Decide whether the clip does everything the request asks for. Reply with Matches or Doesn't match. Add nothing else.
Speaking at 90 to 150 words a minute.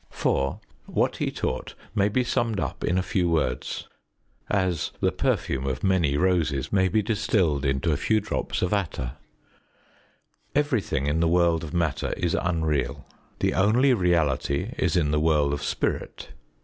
Doesn't match